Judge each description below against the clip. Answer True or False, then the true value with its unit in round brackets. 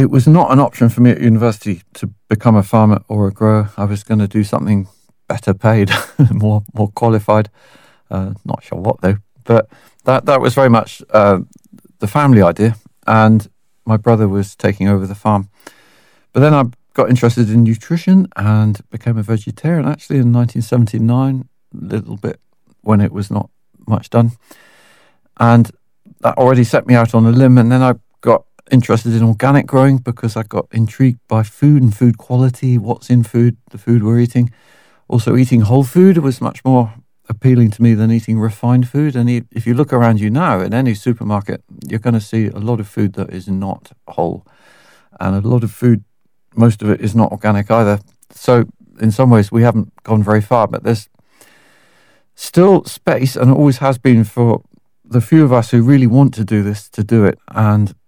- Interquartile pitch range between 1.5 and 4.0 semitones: True (2.8 semitones)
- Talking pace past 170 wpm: True (190 wpm)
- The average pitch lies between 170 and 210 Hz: False (115 Hz)